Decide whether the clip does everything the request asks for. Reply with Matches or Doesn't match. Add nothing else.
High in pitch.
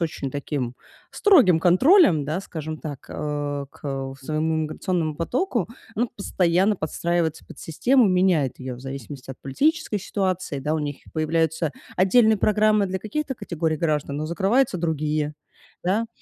Doesn't match